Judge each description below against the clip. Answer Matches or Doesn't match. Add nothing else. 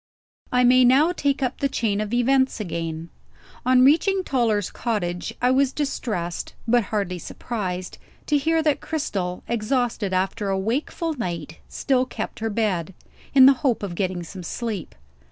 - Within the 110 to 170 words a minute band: Matches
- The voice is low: Doesn't match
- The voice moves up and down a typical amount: Doesn't match